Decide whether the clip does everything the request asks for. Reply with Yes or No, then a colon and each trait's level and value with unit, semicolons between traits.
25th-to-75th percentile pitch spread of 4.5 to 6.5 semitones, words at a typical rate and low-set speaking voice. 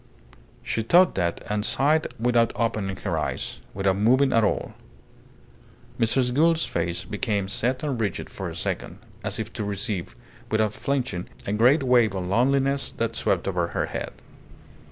Yes: average, 4.8 semitones; average, 155 wpm; low, 110 Hz